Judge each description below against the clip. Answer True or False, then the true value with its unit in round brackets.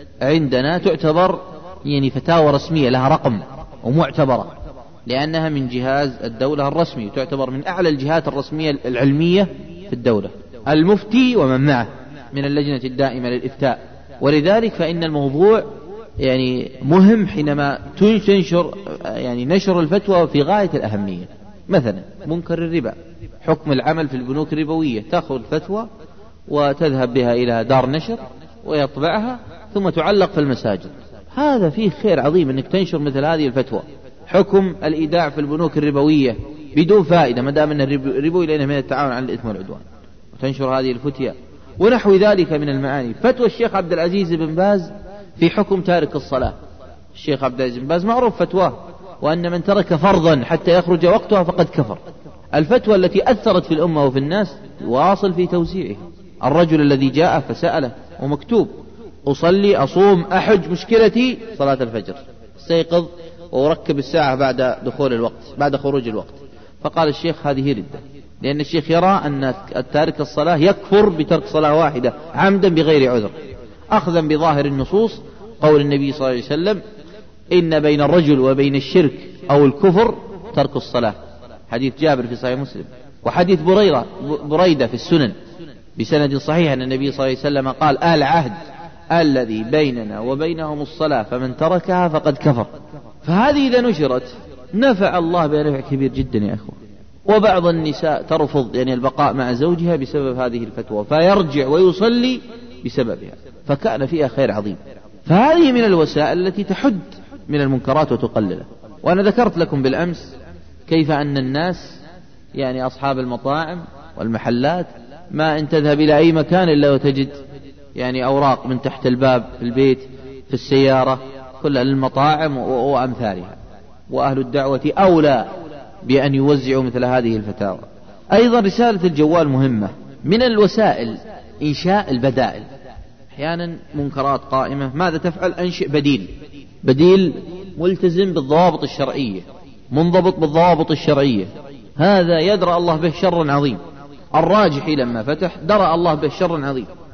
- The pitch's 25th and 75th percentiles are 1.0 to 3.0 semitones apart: False (4.8 semitones)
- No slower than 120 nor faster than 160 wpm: True (130 wpm)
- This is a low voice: False (150 Hz)